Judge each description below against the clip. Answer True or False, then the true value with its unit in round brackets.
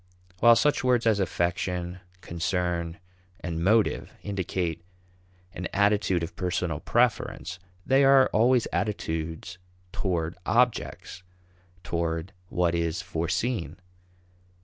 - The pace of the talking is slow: True (100 wpm)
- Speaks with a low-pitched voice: True (90 Hz)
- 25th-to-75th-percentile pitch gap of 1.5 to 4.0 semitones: False (4.5 semitones)